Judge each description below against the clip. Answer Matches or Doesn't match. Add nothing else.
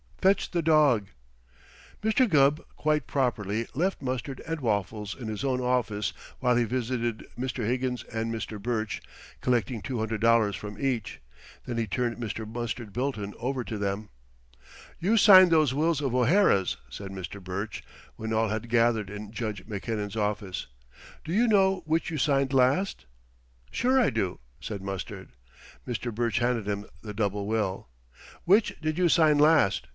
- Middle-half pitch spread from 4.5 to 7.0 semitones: Matches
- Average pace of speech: Matches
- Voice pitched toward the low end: Matches